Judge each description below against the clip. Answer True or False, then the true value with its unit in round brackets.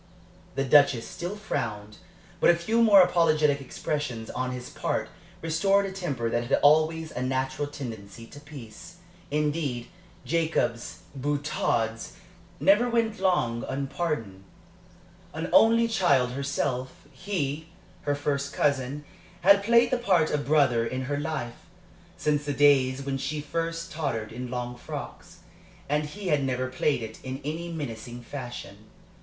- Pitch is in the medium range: True (145 Hz)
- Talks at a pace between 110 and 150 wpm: True (140 wpm)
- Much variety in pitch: False (4.6 semitones)